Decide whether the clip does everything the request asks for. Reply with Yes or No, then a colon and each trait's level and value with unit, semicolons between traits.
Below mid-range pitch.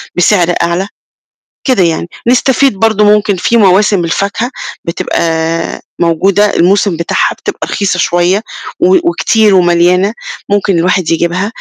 No: high, 190 Hz